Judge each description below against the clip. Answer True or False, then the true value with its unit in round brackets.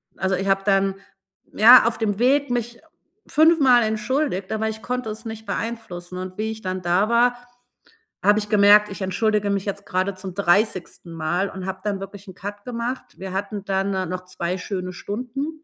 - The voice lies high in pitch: True (205 Hz)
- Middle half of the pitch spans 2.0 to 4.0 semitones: True (3.1 semitones)